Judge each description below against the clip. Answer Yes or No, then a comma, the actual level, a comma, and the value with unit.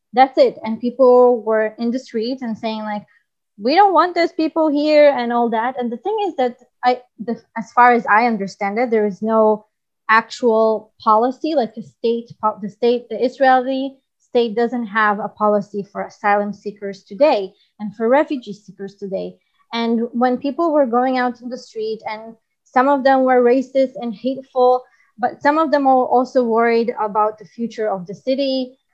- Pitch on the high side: Yes, high, 240 Hz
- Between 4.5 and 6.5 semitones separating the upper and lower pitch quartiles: No, average, 3.3 semitones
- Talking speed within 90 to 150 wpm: No, average, 185 wpm